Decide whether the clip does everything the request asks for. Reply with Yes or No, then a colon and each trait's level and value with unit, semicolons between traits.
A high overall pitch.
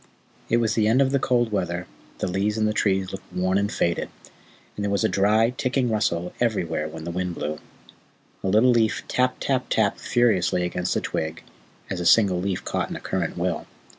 No: low, 100 Hz